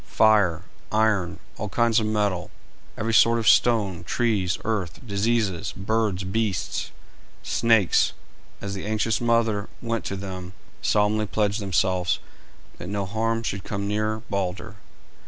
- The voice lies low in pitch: Yes, low, 105 Hz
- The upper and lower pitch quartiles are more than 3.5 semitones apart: No, average, 2.7 semitones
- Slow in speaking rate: Yes, slow, 130 wpm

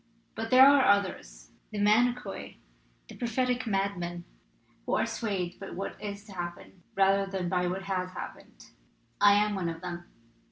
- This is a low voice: No, high, 195 Hz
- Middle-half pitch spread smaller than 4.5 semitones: Yes, average, 2.9 semitones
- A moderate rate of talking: Yes, average, 155 wpm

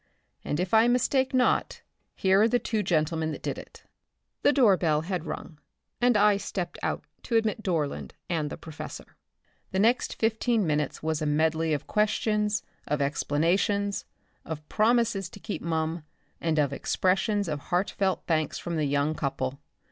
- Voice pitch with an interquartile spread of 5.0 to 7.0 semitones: Yes, wide, 5.5 semitones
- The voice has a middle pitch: Yes, medium, 175 Hz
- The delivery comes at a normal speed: Yes, average, 160 wpm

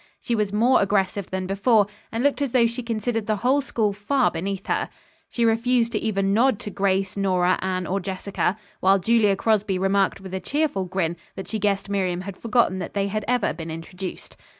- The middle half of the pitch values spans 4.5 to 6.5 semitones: No, average, 3.3 semitones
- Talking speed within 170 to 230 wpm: Yes, average, 200 wpm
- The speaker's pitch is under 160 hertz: No, high, 200 Hz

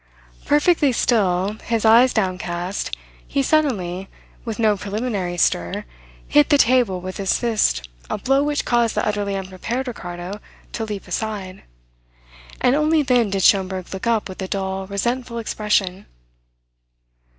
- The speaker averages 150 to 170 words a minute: No, average, 140 wpm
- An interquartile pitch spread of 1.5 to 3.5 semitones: No, average, 4.3 semitones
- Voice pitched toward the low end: No, high, 210 Hz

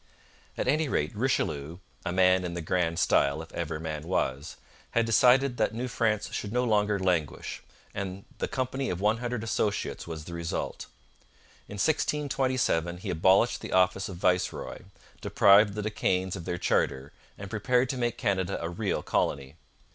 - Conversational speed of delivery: Yes, average, 170 wpm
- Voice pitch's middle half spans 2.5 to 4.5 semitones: No, average, 5.3 semitones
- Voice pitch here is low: Yes, very low, 95 Hz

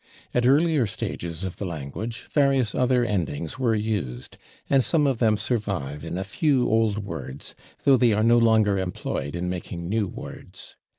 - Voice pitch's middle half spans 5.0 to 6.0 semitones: Yes, wide, 5.6 semitones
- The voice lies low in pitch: Yes, low, 110 Hz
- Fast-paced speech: No, average, 170 wpm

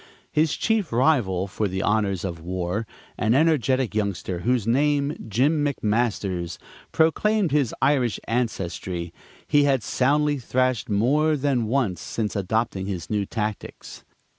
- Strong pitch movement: Yes, wide, 6.2 semitones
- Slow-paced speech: Yes, slow, 130 wpm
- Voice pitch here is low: Yes, low, 115 Hz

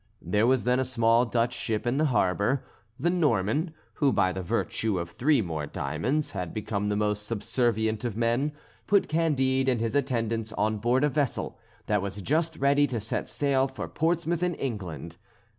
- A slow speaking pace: No, average, 180 wpm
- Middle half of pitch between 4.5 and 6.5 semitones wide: Yes, average, 5.2 semitones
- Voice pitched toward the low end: Yes, low, 120 Hz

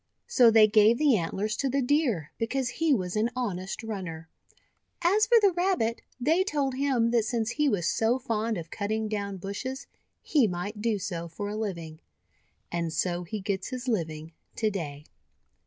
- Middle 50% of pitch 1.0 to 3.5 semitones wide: No, wide, 5.6 semitones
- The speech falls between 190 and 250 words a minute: No, average, 180 wpm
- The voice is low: No, high, 220 Hz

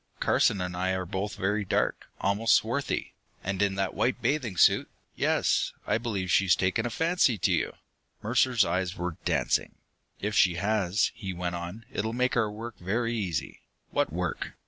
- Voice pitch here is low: Yes, low, 100 Hz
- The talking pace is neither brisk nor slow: Yes, average, 170 wpm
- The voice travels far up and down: No, average, 3.6 semitones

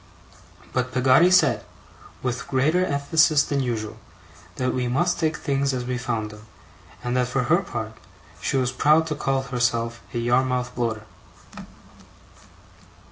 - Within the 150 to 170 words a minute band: No, average, 140 wpm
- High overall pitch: No, low, 130 Hz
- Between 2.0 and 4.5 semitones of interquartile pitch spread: Yes, narrow, 2.6 semitones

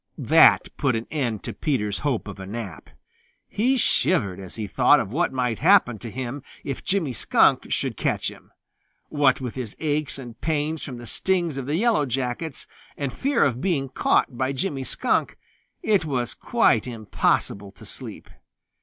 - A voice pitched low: Yes, low, 130 Hz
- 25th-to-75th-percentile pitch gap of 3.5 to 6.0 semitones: Yes, average, 4.8 semitones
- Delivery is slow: No, average, 170 wpm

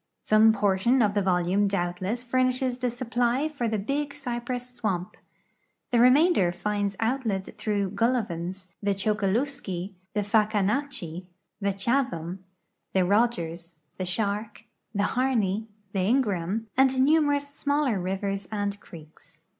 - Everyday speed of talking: No, slow, 120 wpm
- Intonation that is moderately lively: Yes, average, 4.6 semitones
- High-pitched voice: Yes, high, 210 Hz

